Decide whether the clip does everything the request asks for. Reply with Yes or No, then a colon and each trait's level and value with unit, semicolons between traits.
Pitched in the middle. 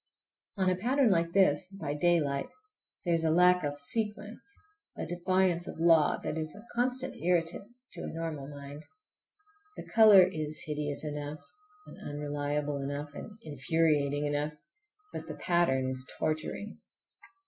Yes: medium, 160 Hz